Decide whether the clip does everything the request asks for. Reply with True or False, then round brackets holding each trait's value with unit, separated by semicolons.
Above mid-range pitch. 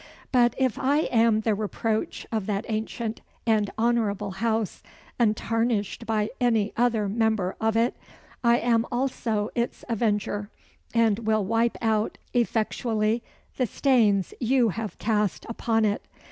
True (225 Hz)